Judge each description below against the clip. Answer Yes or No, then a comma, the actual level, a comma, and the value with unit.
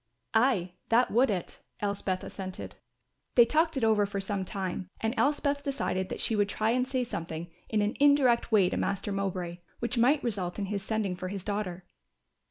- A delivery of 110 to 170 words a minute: No, average, 185 wpm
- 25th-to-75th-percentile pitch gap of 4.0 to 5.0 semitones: Yes, average, 4.3 semitones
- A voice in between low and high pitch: No, high, 205 Hz